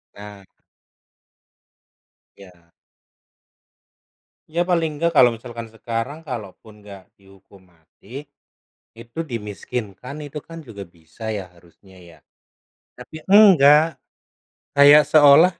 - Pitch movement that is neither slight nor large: No, wide, 6.8 semitones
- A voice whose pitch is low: Yes, low, 115 Hz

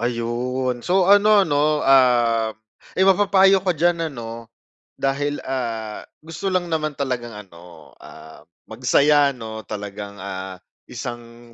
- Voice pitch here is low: Yes, low, 125 Hz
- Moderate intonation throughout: No, wide, 5.9 semitones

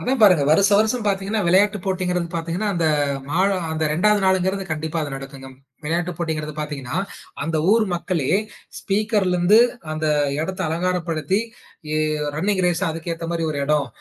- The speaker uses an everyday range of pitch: Yes, average, 3.6 semitones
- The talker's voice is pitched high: No, medium, 175 Hz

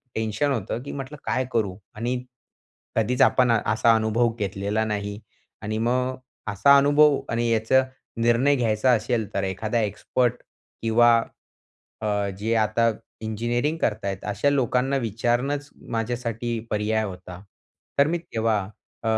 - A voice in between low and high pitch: No, low, 115 Hz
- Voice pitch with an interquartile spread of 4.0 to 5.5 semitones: No, average, 2.9 semitones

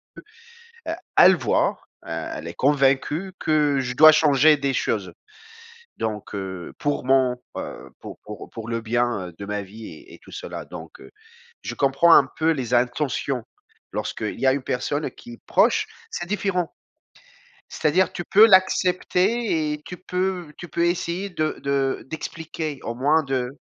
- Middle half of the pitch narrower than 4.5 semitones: No, wide, 5.6 semitones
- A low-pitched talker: No, medium, 145 Hz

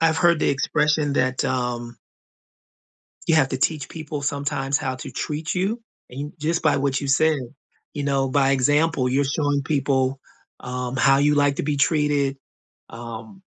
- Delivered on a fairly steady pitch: Yes, narrow, 2.2 semitones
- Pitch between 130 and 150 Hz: Yes, medium, 140 Hz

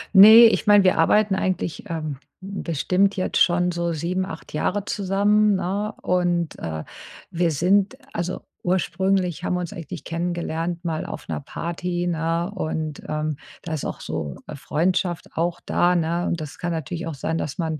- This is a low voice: No, medium, 175 Hz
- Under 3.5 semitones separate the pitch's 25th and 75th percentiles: Yes, narrow, 2.5 semitones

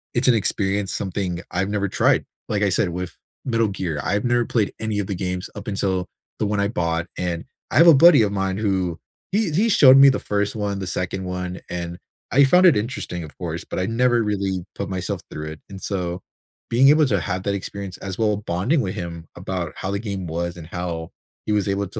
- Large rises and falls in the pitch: No, average, 3.6 semitones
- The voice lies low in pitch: Yes, low, 100 Hz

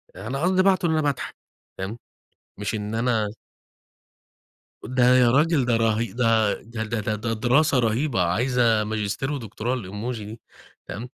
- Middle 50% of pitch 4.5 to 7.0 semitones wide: No, average, 3.0 semitones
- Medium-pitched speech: No, low, 115 Hz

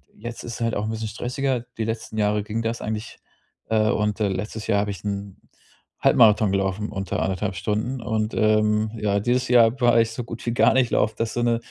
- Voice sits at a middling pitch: No, low, 110 Hz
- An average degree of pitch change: No, narrow, 1.9 semitones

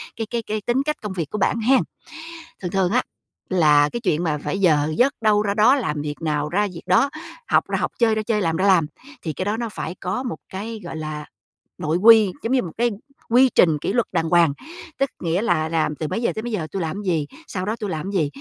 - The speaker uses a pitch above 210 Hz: No, high, 190 Hz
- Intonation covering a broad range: Yes, wide, 5.9 semitones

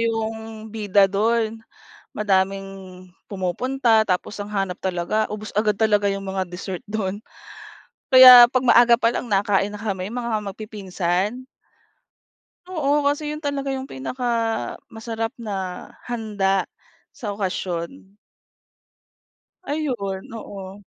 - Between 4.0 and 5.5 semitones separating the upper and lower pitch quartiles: No, average, 3.3 semitones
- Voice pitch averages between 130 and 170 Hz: No, high, 215 Hz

